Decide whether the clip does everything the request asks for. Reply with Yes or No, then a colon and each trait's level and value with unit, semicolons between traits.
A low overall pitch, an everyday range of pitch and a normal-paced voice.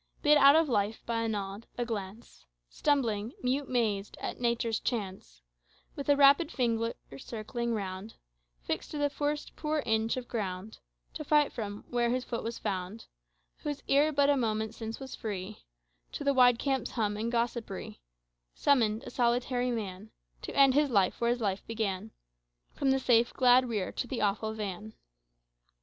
No: high, 235 Hz; average, 3.8 semitones; average, 170 wpm